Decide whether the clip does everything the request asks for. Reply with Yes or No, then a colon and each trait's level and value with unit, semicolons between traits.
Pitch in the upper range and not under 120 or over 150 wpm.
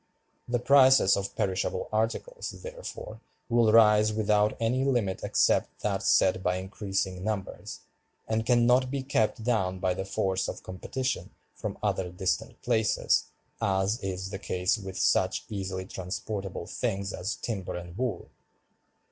No: low, 105 Hz; average, 140 wpm